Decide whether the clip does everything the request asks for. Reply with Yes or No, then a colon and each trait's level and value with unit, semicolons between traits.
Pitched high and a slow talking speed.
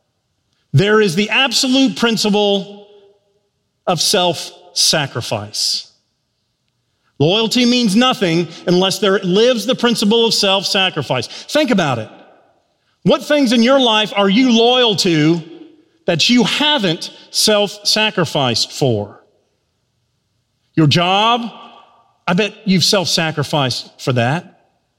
Yes: high, 195 Hz; slow, 110 wpm